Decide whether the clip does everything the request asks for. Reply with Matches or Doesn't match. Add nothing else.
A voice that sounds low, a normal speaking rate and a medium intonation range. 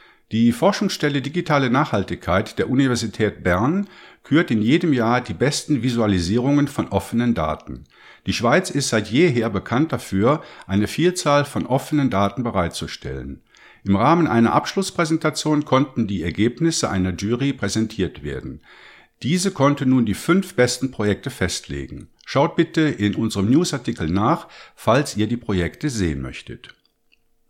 Doesn't match